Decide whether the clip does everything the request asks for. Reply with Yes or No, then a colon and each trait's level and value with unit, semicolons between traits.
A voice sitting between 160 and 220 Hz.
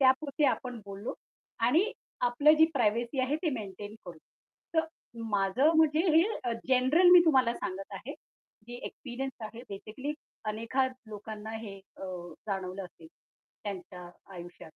No: high, 235 Hz